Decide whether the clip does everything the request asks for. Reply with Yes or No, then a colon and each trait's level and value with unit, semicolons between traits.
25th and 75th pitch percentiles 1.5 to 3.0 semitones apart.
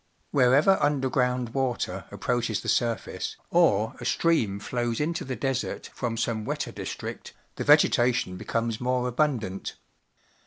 Yes: average, 2.7 semitones